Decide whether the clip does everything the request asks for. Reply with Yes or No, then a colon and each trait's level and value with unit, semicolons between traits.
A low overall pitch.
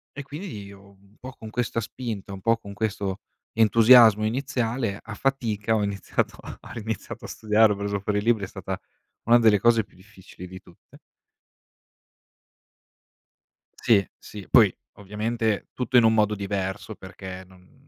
Yes: low, 105 Hz